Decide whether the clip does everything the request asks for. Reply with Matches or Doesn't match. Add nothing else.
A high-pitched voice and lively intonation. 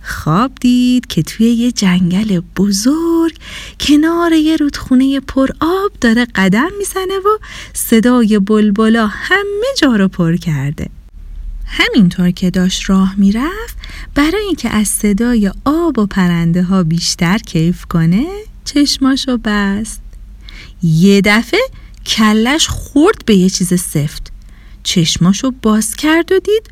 Matches